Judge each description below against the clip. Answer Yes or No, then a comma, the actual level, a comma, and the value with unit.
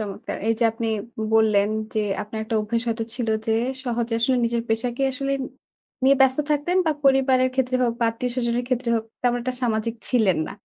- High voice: Yes, high, 235 Hz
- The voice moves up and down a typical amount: No, narrow, 2.3 semitones